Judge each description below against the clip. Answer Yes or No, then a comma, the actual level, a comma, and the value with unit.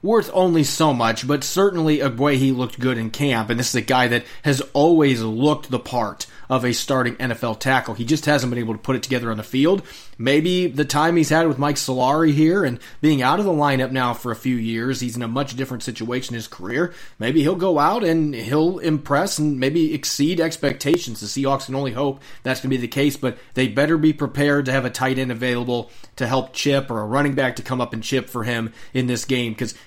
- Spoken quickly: Yes, fast, 240 wpm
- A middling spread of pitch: Yes, average, 3.3 semitones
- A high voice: No, low, 130 Hz